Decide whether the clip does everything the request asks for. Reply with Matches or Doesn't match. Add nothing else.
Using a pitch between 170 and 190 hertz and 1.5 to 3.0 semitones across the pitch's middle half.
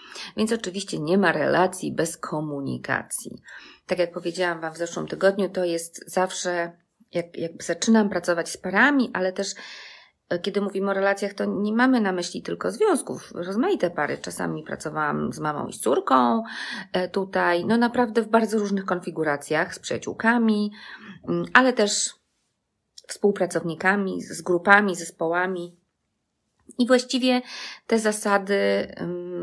Doesn't match